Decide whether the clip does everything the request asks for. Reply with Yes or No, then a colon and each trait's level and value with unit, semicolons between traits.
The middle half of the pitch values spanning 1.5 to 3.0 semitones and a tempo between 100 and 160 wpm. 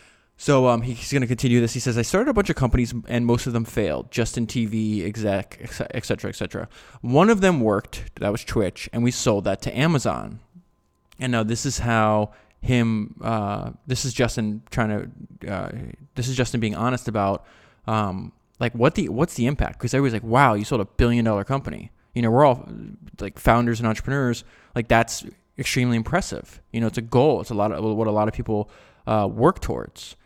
No: average, 2.7 semitones; fast, 205 wpm